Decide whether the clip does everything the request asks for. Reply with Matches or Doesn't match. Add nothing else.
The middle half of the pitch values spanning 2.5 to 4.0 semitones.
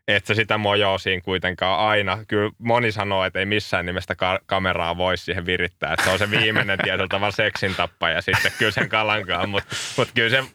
Matches